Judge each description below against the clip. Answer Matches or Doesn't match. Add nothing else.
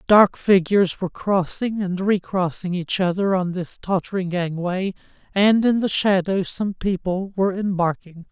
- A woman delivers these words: Doesn't match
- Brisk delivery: Doesn't match